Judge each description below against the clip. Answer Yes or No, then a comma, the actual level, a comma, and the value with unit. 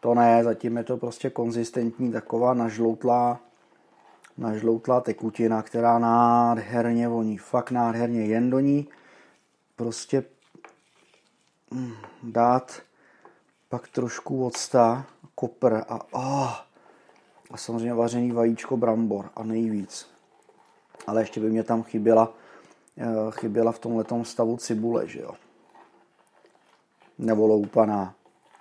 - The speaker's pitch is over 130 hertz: No, low, 115 Hz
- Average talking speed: No, slow, 105 wpm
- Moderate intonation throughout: No, narrow, 1.1 semitones